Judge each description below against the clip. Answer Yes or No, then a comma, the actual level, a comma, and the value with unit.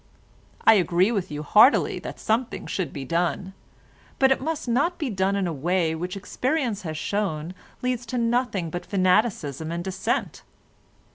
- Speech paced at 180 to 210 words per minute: No, average, 160 wpm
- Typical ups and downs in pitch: No, wide, 5.8 semitones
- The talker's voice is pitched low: No, high, 190 Hz